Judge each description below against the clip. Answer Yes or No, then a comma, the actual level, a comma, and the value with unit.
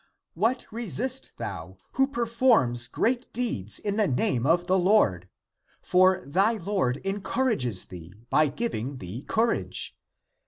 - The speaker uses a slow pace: Yes, slow, 130 wpm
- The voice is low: No, medium, 185 Hz